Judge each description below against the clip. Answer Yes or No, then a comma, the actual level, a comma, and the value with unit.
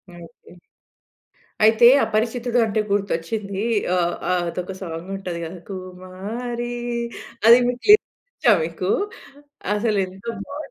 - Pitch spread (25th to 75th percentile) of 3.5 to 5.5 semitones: Yes, average, 4.3 semitones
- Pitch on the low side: No, high, 200 Hz